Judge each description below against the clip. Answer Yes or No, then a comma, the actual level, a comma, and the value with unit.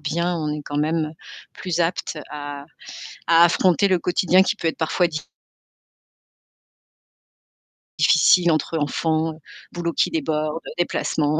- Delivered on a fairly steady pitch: Yes, narrow, 2.2 semitones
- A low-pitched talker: No, medium, 160 Hz